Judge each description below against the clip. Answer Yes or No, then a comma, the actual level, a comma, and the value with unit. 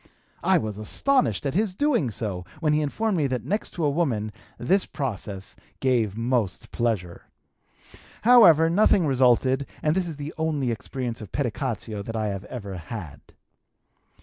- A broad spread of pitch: Yes, wide, 6.8 semitones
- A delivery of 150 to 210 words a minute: Yes, average, 155 wpm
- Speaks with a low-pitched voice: Yes, low, 130 Hz